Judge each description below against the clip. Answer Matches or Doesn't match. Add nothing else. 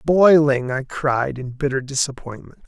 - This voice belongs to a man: Matches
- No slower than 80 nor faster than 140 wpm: Matches